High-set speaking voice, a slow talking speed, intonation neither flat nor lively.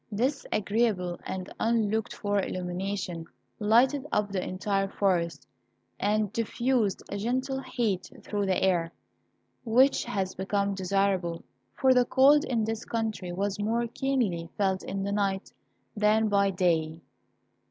Yes: high, 205 Hz; slow, 130 wpm; average, 3.4 semitones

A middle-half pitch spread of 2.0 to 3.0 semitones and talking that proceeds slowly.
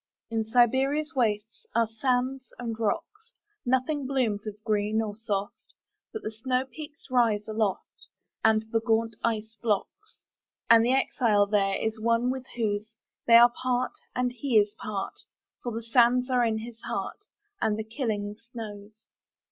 Yes: average, 2.7 semitones; slow, 125 wpm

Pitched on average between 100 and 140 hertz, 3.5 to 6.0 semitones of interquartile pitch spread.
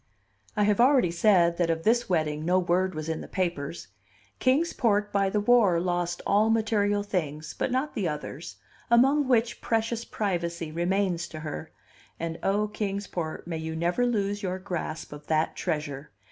No: medium, 185 Hz; average, 4.3 semitones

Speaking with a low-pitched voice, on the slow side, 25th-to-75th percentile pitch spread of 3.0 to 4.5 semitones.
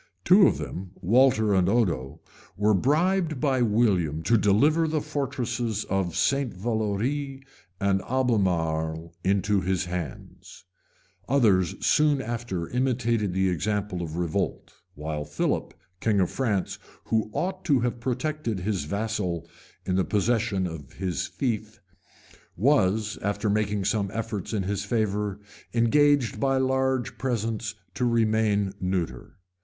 No: low, 105 Hz; slow, 130 wpm; average, 5.0 semitones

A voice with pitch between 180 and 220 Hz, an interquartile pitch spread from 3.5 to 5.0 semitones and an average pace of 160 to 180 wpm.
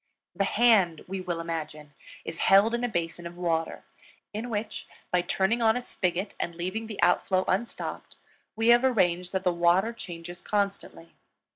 Yes: medium, 185 Hz; average, 4.3 semitones; average, 165 wpm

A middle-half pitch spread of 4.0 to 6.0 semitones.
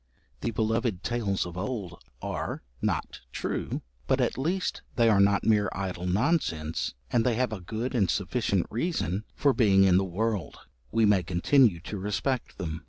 Yes: average, 4.3 semitones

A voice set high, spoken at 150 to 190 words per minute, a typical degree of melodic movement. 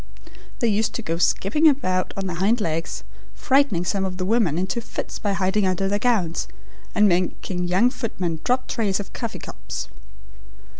Yes: high, 195 Hz; average, 170 wpm; average, 4.0 semitones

